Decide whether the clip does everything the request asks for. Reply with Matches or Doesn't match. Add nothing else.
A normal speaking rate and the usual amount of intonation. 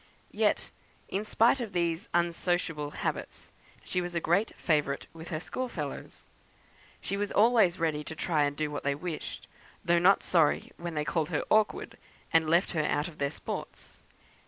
Matches